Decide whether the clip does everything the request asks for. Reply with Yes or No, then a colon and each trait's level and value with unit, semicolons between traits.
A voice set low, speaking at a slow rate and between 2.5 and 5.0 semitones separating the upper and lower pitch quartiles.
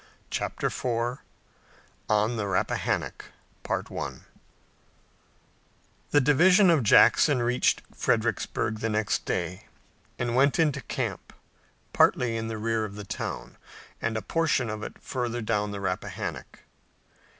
Yes: low, 115 Hz; slow, 115 wpm; average, 3.3 semitones